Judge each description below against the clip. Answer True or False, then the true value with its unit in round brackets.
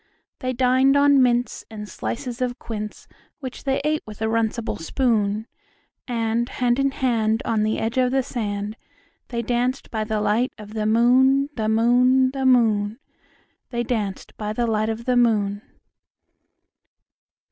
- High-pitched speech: True (235 Hz)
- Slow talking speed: False (155 wpm)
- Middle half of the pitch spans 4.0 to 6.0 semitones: False (2.8 semitones)